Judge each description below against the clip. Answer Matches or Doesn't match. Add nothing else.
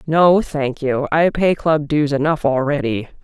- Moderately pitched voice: Matches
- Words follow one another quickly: Doesn't match